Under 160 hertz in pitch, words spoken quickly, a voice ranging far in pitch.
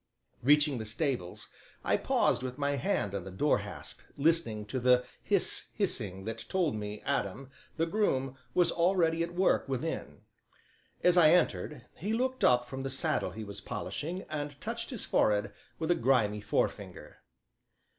No: low, 135 Hz; average, 160 wpm; wide, 6.7 semitones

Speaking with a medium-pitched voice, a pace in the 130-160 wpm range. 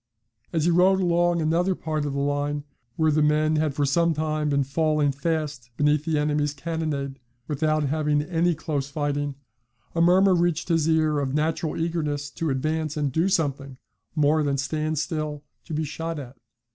No: medium, 155 Hz; average, 175 wpm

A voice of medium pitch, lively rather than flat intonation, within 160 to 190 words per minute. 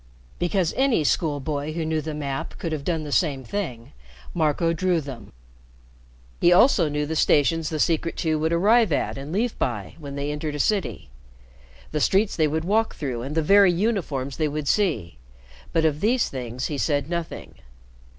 No: medium, 155 Hz; average, 3.6 semitones; average, 185 wpm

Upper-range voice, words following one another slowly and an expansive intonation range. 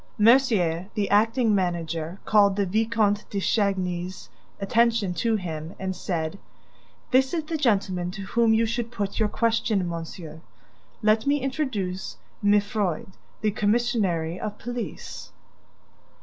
No: high, 205 Hz; slow, 125 wpm; average, 4.0 semitones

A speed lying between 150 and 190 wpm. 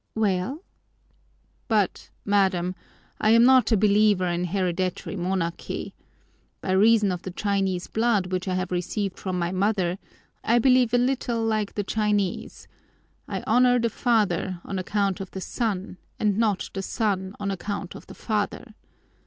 Yes: average, 155 wpm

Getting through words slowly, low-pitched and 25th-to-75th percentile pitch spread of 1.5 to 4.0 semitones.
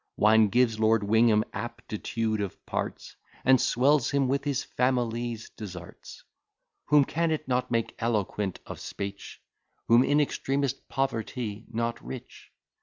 Yes: slow, 130 wpm; low, 115 Hz; average, 3.4 semitones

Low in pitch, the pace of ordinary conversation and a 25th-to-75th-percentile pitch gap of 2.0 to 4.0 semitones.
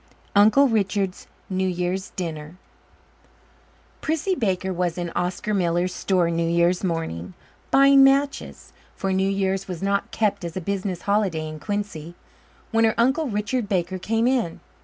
No: high, 190 Hz; average, 145 wpm; average, 3.6 semitones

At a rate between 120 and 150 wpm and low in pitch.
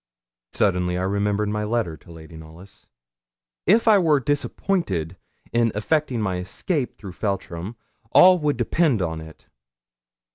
Yes: slow, 135 wpm; low, 105 Hz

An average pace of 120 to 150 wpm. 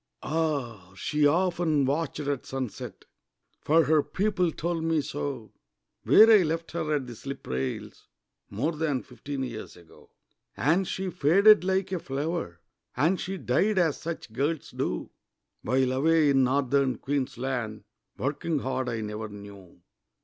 Yes: average, 140 wpm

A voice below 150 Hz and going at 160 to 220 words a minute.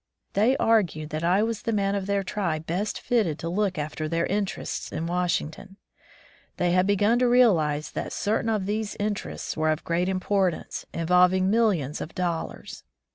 No: medium, 185 Hz; average, 170 wpm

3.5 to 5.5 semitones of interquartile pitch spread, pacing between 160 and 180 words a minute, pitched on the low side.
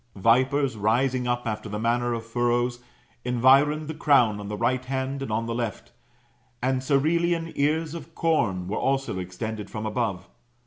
Yes: average, 3.8 semitones; average, 165 wpm; low, 120 Hz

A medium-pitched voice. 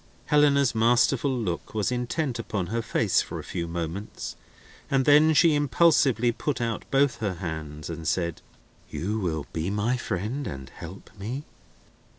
No: low, 115 Hz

